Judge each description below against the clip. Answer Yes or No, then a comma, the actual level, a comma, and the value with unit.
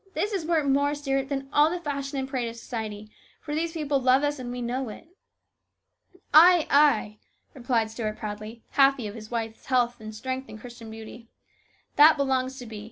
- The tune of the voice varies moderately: Yes, average, 4.1 semitones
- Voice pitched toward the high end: Yes, very high, 260 Hz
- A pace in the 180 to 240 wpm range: Yes, average, 200 wpm